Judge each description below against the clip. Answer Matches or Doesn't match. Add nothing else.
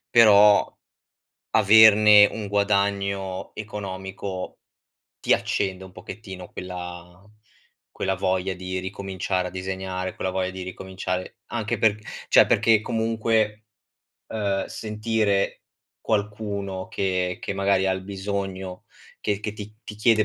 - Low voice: Matches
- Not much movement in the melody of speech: Matches